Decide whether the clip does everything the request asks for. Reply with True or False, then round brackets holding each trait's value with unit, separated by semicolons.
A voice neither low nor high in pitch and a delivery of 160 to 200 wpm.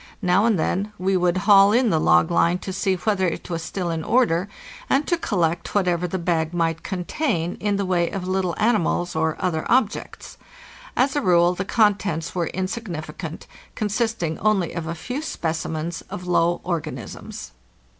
True (180 Hz; 170 wpm)